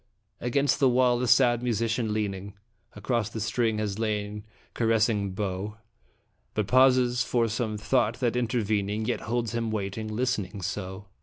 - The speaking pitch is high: No, low, 110 Hz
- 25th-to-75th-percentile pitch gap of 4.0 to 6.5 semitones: No, average, 2.7 semitones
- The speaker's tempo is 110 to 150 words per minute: Yes, average, 145 wpm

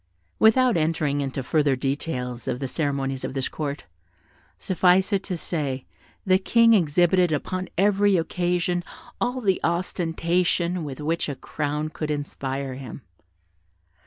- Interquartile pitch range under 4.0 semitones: No, average, 4.6 semitones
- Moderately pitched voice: Yes, medium, 165 Hz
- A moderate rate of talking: No, slow, 130 wpm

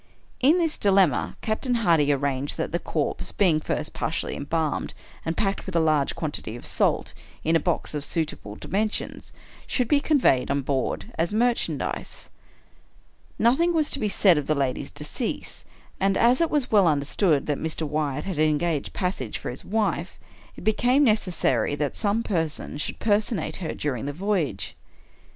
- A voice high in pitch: No, medium, 165 Hz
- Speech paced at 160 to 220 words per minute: Yes, average, 165 wpm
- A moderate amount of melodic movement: No, wide, 6.6 semitones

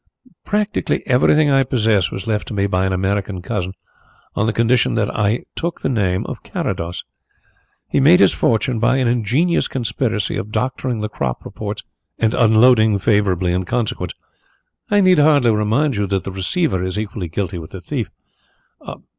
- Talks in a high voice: No, low, 110 Hz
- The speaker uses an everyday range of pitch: Yes, average, 4.8 semitones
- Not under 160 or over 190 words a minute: Yes, average, 170 wpm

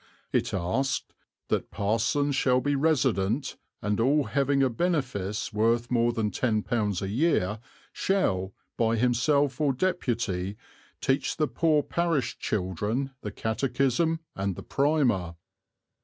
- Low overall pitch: Yes, low, 125 Hz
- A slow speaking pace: Yes, slow, 125 wpm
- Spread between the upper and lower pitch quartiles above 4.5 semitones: Yes, average, 5.2 semitones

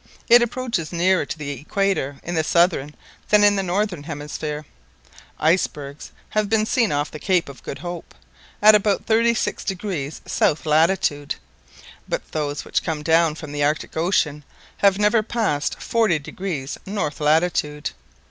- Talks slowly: No, average, 155 wpm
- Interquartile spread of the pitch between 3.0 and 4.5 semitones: No, average, 5.3 semitones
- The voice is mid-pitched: Yes, medium, 170 Hz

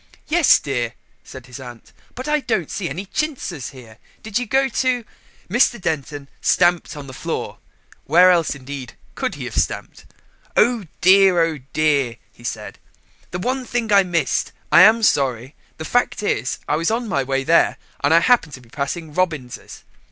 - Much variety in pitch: Yes, wide, 8.0 semitones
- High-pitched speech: No, medium, 165 Hz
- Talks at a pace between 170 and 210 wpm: Yes, average, 180 wpm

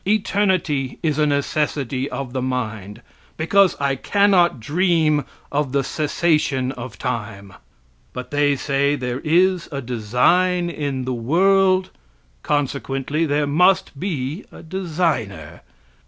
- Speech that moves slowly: Yes, slow, 120 wpm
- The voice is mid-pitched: Yes, medium, 145 Hz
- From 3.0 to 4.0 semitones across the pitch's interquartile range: No, average, 5.1 semitones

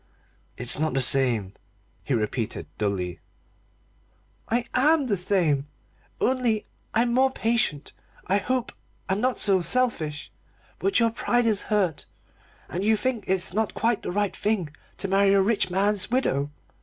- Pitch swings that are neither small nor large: No, wide, 7.3 semitones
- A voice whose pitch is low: No, high, 200 Hz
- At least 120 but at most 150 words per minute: Yes, average, 145 wpm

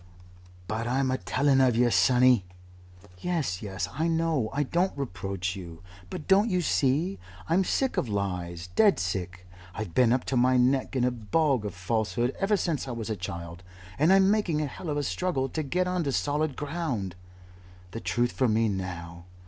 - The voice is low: Yes, low, 125 Hz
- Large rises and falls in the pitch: Yes, wide, 8.1 semitones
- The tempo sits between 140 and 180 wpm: No, average, 190 wpm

